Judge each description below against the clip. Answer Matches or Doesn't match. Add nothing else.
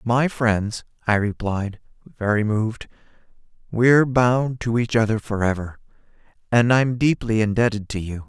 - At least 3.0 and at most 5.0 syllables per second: Matches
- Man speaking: Matches